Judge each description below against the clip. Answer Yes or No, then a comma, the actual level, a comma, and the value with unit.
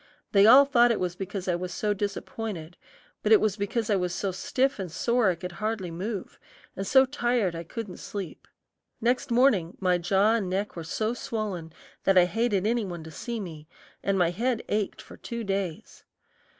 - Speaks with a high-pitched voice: Yes, high, 200 Hz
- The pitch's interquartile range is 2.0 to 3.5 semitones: No, average, 4.0 semitones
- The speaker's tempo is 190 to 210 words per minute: Yes, average, 195 wpm